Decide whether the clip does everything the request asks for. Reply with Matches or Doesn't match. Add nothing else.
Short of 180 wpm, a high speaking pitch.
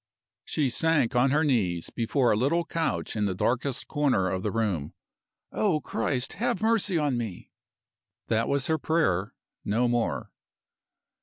Doesn't match